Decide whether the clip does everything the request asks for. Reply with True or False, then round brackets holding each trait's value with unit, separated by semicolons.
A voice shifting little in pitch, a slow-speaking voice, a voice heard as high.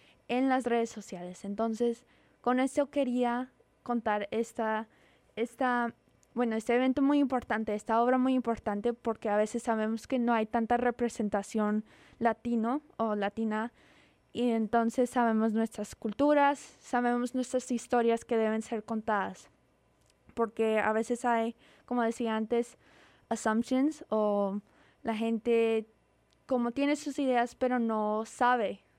True (1.8 semitones; 130 wpm; 235 Hz)